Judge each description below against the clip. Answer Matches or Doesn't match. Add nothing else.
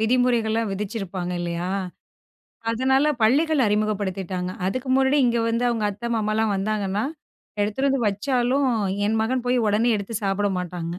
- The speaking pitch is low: Doesn't match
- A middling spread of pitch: Matches